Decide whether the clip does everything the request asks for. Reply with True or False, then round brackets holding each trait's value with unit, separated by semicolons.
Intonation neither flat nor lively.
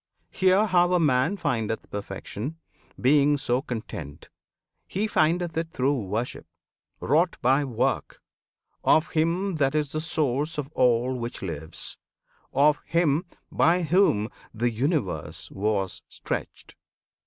False (6.1 semitones)